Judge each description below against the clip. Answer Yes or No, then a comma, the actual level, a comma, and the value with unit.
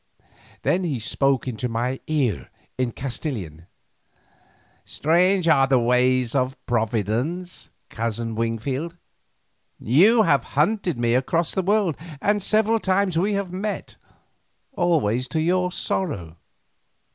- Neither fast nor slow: No, slow, 115 wpm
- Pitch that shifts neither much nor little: No, wide, 7.3 semitones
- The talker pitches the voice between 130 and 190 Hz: Yes, medium, 140 Hz